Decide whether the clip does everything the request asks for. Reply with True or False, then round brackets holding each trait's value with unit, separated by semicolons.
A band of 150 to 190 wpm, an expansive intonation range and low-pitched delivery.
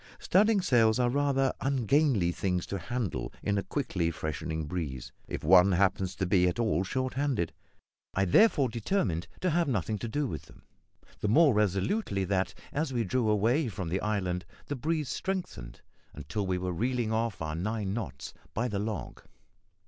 True (170 wpm; 6.2 semitones; 105 Hz)